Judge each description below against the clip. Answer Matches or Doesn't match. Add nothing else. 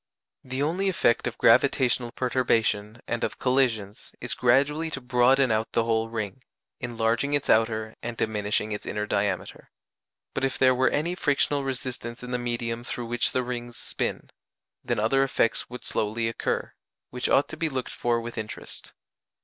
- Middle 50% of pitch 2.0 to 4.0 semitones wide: Matches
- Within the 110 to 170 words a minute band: Matches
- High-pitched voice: Doesn't match